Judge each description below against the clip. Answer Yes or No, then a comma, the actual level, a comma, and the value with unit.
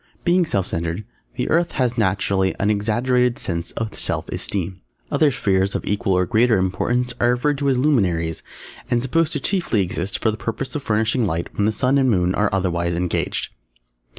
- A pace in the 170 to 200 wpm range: Yes, average, 185 wpm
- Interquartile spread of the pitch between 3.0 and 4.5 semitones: No, average, 5.0 semitones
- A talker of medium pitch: No, low, 105 Hz